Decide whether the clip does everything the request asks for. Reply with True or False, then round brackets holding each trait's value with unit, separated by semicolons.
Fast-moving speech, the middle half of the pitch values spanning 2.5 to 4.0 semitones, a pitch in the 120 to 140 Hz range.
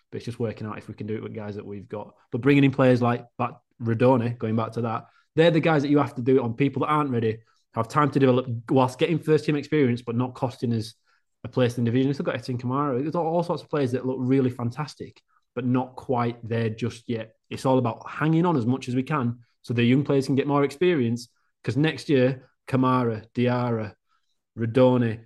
True (240 wpm; 3.1 semitones; 125 Hz)